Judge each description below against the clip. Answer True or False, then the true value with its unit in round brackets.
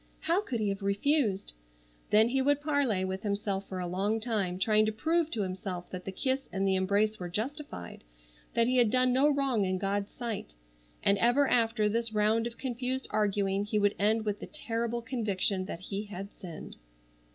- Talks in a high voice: True (215 Hz)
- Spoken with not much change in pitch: False (4.0 semitones)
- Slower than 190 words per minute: False (195 wpm)